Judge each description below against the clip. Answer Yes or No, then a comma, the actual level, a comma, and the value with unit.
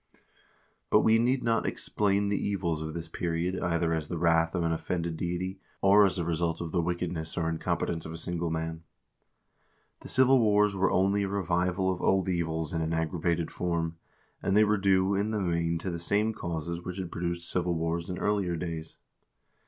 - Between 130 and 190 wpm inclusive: No, average, 200 wpm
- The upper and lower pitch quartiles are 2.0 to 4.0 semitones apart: Yes, average, 2.7 semitones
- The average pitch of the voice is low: Yes, very low, 85 Hz